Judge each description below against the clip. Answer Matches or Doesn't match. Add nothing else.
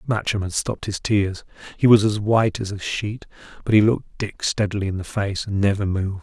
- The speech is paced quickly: Matches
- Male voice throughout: Matches